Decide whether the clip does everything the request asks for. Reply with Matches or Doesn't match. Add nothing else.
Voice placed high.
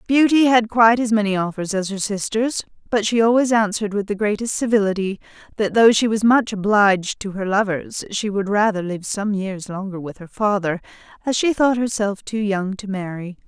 Matches